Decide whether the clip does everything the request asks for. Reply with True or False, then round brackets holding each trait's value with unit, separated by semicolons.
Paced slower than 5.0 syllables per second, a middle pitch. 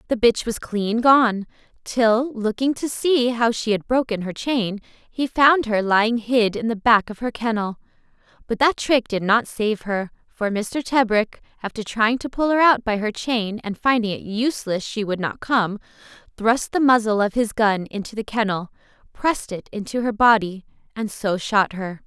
False (4.6 syllables/s; 225 Hz)